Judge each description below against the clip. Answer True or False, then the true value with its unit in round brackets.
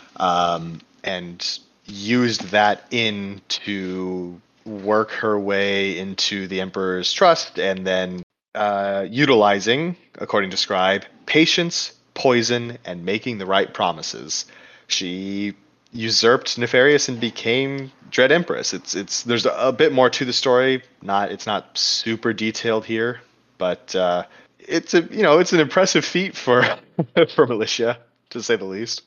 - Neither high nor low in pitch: False (110 Hz)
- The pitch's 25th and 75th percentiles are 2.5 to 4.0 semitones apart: False (4.7 semitones)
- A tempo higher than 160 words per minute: False (140 wpm)